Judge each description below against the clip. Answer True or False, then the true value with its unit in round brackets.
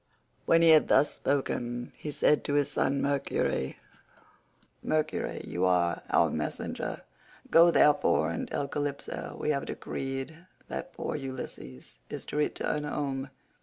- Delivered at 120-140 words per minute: True (135 wpm)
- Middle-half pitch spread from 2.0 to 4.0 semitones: True (2.4 semitones)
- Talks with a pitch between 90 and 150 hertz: True (140 Hz)